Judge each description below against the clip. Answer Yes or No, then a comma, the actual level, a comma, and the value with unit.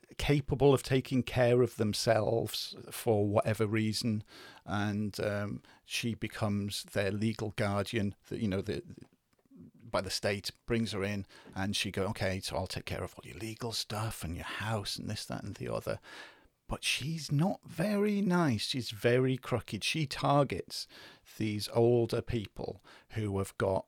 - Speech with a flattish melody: No, average, 3.4 semitones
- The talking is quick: No, average, 165 wpm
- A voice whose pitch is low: Yes, low, 110 Hz